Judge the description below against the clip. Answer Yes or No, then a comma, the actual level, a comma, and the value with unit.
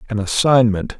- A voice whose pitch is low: Yes, low, 115 Hz